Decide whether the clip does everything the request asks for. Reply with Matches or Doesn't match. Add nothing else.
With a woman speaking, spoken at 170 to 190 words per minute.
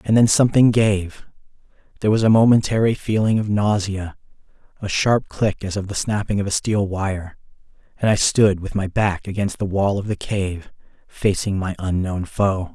Doesn't match